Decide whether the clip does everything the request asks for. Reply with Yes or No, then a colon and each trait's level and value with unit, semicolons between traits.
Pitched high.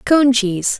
Yes: high, 235 Hz